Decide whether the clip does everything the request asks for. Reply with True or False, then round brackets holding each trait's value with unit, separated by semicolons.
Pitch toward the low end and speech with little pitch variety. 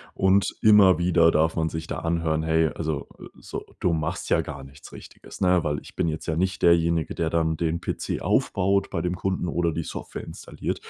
True (85 Hz; 1.9 semitones)